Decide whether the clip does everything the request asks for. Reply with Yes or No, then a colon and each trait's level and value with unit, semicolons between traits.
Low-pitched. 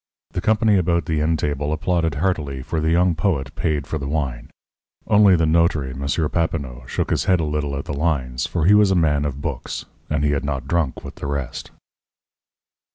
Yes: very low, 75 Hz